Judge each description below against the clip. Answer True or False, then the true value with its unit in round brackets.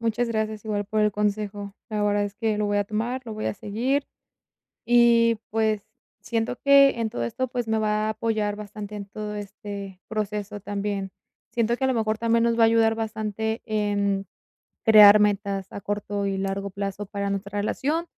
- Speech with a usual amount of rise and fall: False (1.8 semitones)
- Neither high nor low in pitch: False (210 Hz)